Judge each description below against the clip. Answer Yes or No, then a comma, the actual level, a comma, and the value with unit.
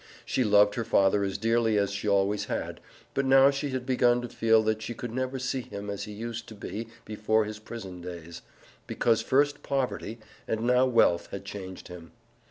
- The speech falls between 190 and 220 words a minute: Yes, average, 195 wpm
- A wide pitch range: No, average, 3.4 semitones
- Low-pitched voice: Yes, low, 110 Hz